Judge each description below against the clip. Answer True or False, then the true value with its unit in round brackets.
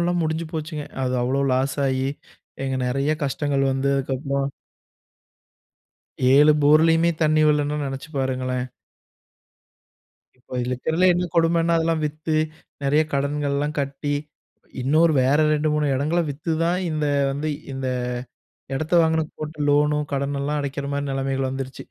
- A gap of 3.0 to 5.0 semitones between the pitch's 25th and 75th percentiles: False (2.4 semitones)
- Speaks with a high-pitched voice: False (145 Hz)